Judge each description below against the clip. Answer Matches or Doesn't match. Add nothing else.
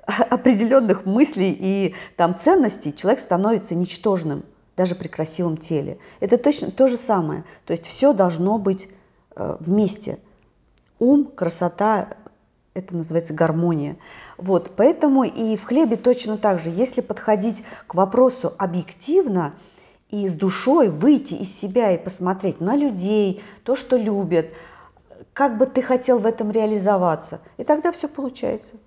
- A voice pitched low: Doesn't match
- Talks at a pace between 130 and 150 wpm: Matches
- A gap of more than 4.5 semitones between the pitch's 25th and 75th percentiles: Matches